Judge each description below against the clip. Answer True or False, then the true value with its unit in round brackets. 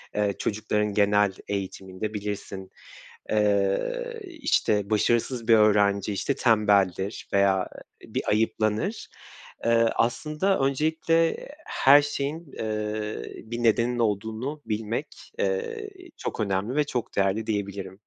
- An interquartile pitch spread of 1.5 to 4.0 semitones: False (5.1 semitones)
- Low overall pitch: True (110 Hz)